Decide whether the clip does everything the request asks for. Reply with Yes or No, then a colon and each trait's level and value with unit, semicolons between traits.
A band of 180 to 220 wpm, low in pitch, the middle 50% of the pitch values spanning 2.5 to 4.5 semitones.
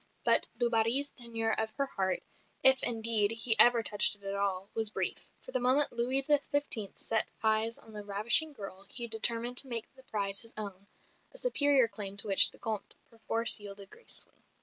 No: average, 190 wpm; high, 225 Hz; average, 3.3 semitones